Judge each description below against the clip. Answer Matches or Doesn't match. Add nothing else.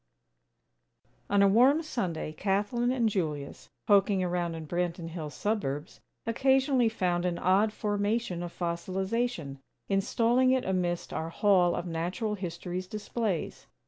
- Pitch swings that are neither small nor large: Matches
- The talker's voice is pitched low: Doesn't match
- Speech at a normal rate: Doesn't match